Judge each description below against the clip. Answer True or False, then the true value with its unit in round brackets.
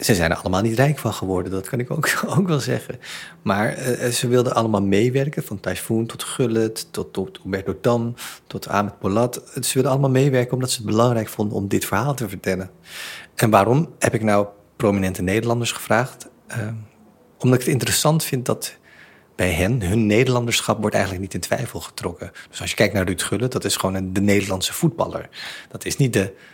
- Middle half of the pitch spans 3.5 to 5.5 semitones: True (4.3 semitones)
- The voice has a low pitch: True (115 Hz)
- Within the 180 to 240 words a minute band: True (200 wpm)